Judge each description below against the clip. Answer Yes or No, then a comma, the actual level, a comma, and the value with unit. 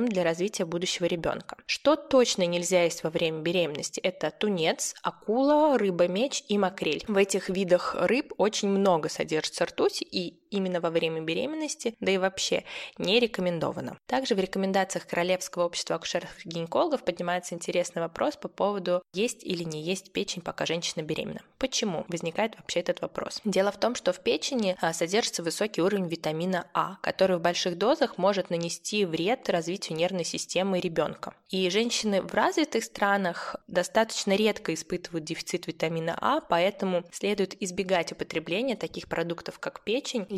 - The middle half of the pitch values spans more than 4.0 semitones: No, average, 3.4 semitones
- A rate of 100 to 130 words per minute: No, average, 150 wpm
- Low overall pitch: No, medium, 185 Hz